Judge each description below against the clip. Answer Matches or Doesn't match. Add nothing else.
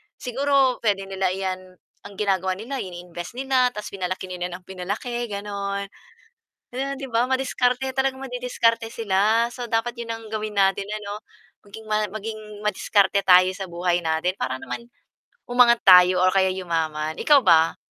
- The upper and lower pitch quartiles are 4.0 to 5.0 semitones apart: Matches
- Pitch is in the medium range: Doesn't match